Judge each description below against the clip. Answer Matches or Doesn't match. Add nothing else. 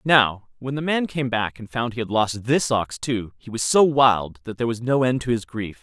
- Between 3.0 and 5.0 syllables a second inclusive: Matches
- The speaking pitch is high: Doesn't match